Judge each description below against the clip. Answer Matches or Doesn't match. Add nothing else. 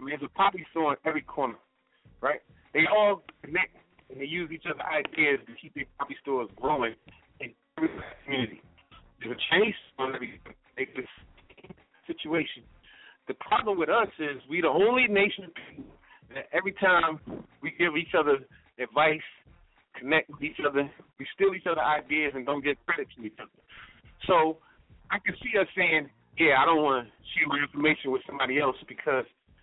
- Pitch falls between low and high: Matches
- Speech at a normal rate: Matches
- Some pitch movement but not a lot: Matches